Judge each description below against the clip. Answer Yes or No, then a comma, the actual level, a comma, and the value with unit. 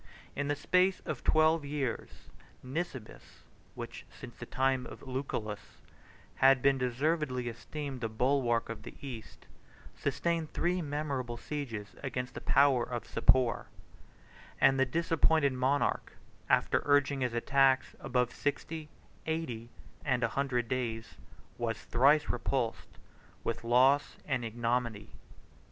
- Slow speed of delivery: Yes, slow, 125 wpm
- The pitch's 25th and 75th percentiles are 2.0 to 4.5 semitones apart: Yes, average, 3.1 semitones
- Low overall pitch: Yes, low, 130 Hz